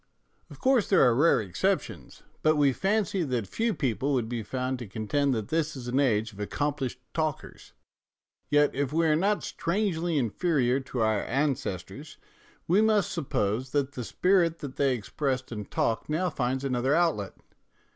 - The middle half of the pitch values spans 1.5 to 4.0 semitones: No, average, 5.3 semitones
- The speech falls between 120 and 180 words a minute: Yes, average, 165 wpm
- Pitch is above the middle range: No, medium, 140 Hz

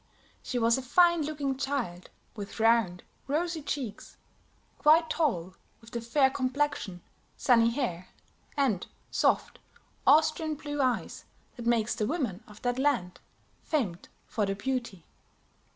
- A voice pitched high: Yes, high, 245 Hz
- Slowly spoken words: Yes, slow, 130 wpm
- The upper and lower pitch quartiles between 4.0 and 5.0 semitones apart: No, wide, 5.4 semitones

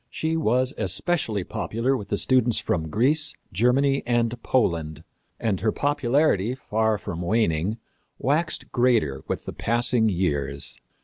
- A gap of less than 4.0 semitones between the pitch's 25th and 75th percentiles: No, wide, 5.6 semitones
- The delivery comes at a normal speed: No, slow, 130 wpm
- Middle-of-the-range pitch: No, low, 115 Hz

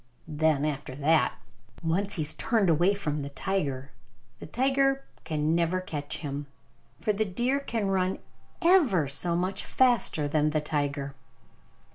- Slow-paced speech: No, average, 145 wpm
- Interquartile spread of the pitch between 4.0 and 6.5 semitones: Yes, wide, 5.4 semitones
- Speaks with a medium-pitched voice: Yes, medium, 170 Hz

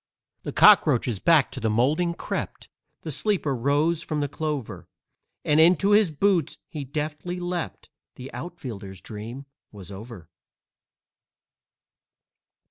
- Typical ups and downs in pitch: No, wide, 6.1 semitones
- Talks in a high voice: No, medium, 150 Hz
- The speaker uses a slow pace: Yes, slow, 120 wpm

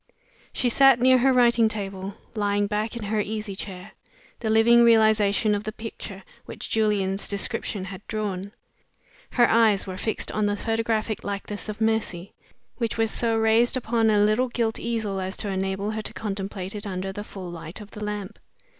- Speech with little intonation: Yes, narrow, 2.2 semitones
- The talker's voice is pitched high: Yes, high, 215 Hz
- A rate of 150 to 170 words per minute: No, average, 180 wpm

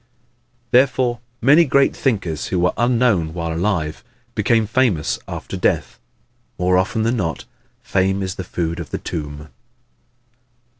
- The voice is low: Yes, very low, 95 Hz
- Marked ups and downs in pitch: Yes, wide, 6.3 semitones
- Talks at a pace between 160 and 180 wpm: No, slow, 135 wpm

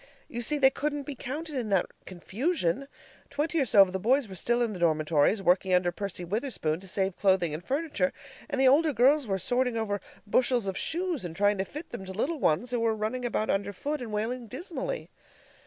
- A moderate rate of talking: No, fast, 215 wpm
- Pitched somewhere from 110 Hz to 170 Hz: No, high, 230 Hz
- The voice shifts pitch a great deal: Yes, wide, 6.4 semitones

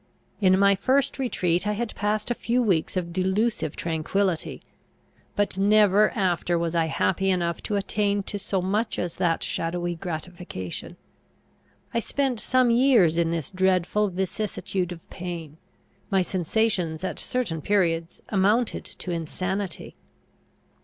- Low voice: No, high, 190 Hz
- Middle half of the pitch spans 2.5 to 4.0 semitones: Yes, average, 3.5 semitones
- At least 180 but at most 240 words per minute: No, slow, 135 wpm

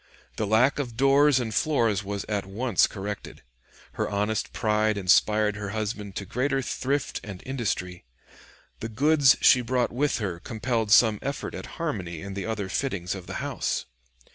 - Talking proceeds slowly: No, average, 165 wpm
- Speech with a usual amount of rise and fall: Yes, average, 4.3 semitones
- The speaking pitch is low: Yes, low, 110 Hz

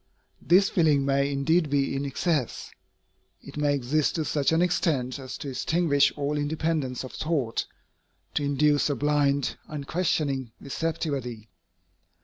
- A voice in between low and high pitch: Yes, medium, 145 Hz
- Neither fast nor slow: No, slow, 130 wpm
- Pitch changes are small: Yes, narrow, 2.3 semitones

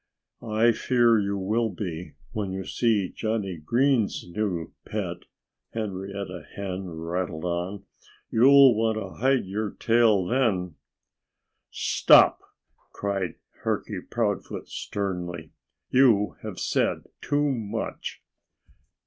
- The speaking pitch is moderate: No, low, 100 Hz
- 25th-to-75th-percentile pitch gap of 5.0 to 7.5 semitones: No, average, 3.8 semitones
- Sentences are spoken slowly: Yes, slow, 105 wpm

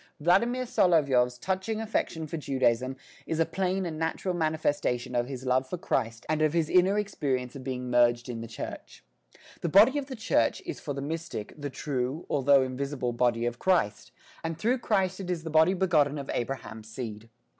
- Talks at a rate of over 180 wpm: Yes, average, 190 wpm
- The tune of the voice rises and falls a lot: Yes, wide, 6.2 semitones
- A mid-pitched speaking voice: Yes, medium, 145 Hz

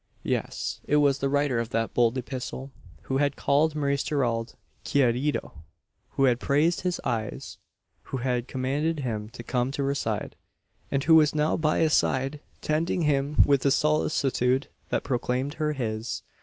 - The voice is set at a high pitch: No, low, 135 Hz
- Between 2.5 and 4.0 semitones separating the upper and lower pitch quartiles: Yes, average, 3.1 semitones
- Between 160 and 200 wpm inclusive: Yes, average, 165 wpm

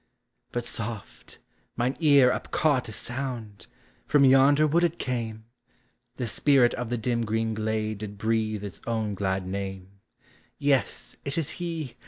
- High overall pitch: No, low, 120 Hz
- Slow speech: No, average, 155 wpm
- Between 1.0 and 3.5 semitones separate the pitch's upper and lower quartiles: No, average, 4.1 semitones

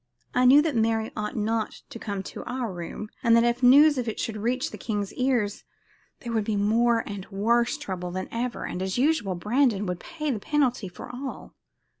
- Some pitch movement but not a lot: Yes, average, 3.6 semitones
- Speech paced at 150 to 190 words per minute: No, fast, 205 wpm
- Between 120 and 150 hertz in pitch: No, high, 230 Hz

